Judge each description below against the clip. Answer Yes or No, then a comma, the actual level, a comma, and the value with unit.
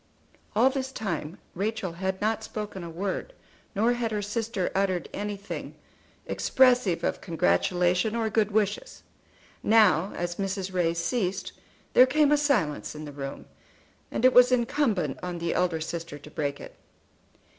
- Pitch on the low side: No, high, 195 Hz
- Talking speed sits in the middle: Yes, average, 150 wpm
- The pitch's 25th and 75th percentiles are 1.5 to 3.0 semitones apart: No, average, 4.8 semitones